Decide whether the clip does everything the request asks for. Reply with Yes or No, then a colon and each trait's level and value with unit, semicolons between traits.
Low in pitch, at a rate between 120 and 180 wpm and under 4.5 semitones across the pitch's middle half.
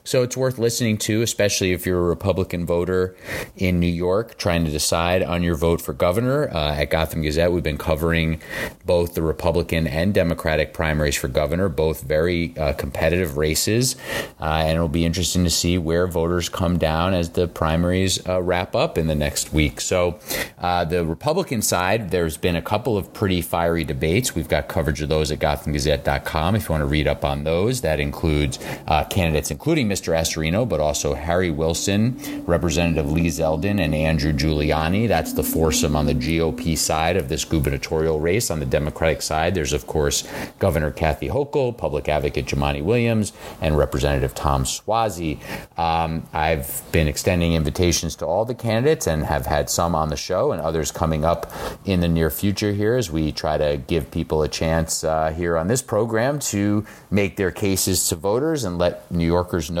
No: very low, 85 Hz; average, 190 wpm; average, 2.8 semitones